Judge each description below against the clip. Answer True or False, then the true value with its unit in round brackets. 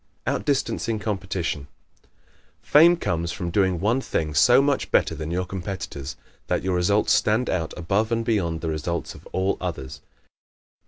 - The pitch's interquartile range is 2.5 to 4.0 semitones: False (4.6 semitones)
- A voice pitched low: True (95 Hz)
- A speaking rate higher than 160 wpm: False (155 wpm)